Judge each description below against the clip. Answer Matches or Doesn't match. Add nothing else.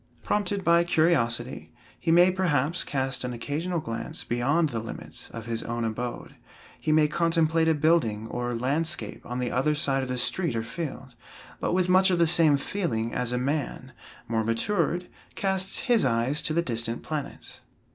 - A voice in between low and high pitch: Matches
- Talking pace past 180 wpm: Doesn't match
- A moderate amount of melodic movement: Doesn't match